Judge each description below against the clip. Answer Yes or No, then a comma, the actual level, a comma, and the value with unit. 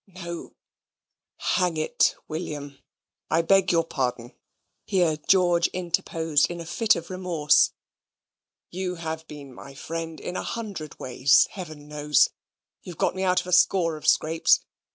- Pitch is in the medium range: Yes, medium, 165 Hz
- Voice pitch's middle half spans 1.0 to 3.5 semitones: Yes, average, 3.1 semitones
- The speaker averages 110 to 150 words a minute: Yes, average, 145 wpm